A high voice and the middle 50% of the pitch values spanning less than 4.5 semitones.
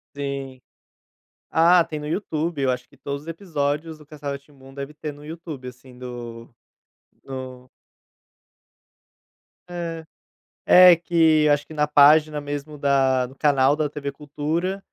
No: medium, 145 Hz; average, 2.7 semitones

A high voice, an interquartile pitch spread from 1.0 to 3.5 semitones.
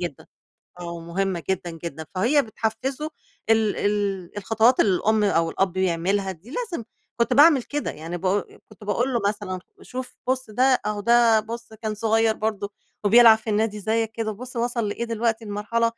Yes: high, 220 Hz; average, 3.2 semitones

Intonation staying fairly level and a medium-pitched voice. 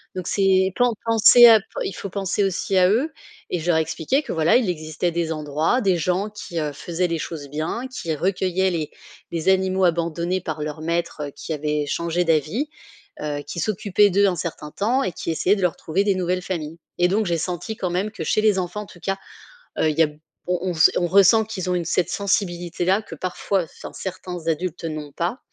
No: average, 3.1 semitones; medium, 180 Hz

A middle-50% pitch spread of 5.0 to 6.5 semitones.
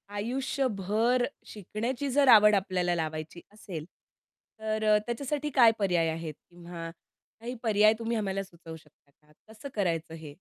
Yes: wide, 5.5 semitones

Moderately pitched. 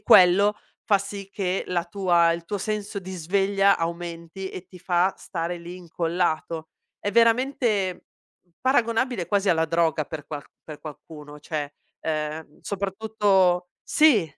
Yes: medium, 180 Hz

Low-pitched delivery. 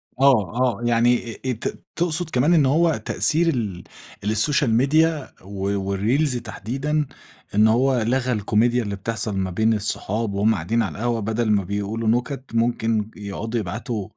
Yes: low, 115 Hz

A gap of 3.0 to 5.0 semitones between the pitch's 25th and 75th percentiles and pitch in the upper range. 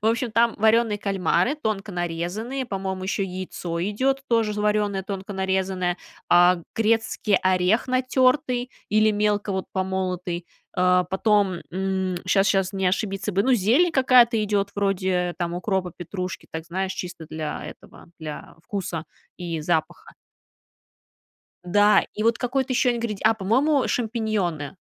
Yes: average, 3.5 semitones; high, 195 Hz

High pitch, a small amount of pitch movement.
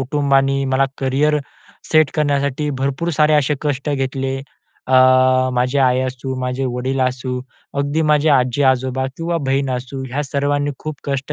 No: low, 135 Hz; narrow, 1.8 semitones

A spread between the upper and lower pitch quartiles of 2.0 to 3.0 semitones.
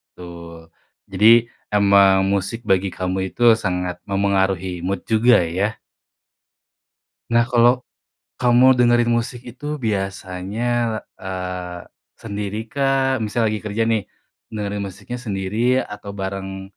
No: average, 3.6 semitones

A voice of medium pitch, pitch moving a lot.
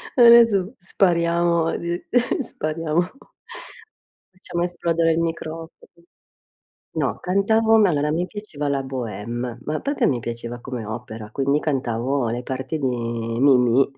Yes: medium, 150 Hz; wide, 5.9 semitones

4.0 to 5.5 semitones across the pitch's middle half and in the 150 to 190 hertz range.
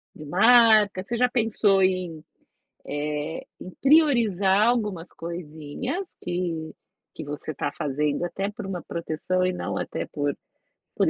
Yes: average, 5.1 semitones; medium, 185 Hz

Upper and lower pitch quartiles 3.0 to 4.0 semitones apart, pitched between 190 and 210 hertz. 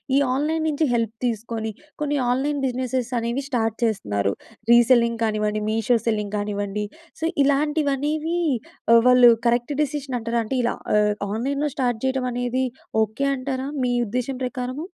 No: average, 3.5 semitones; high, 245 Hz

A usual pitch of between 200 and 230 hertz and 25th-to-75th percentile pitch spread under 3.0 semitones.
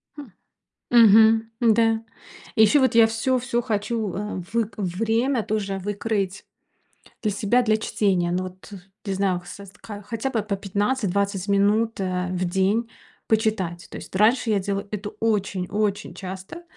Yes: high, 210 Hz; narrow, 2.6 semitones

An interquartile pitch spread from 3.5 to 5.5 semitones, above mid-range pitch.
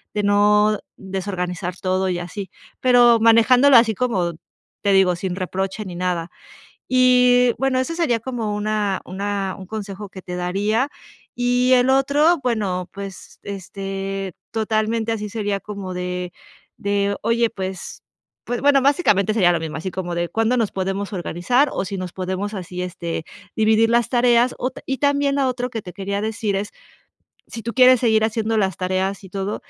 Yes: average, 4.0 semitones; high, 205 Hz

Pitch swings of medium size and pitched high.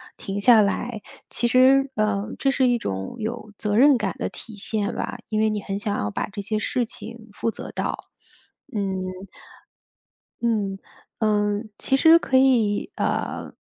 Yes: average, 3.0 semitones; high, 215 Hz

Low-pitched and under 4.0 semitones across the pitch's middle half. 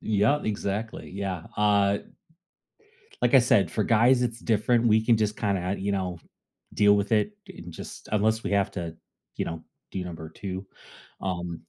Yes: low, 100 Hz; average, 3.1 semitones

